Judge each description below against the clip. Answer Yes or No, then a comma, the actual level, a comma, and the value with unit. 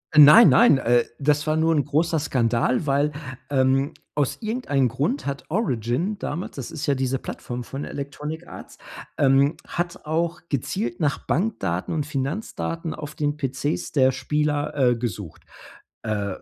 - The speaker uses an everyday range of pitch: Yes, average, 3.4 semitones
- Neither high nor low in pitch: Yes, medium, 145 Hz